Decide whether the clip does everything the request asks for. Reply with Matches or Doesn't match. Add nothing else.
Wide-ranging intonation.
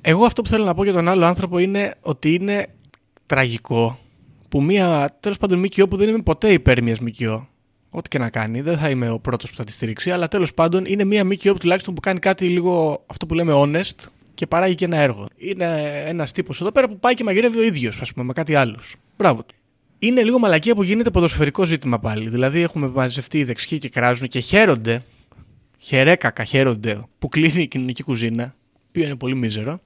Matches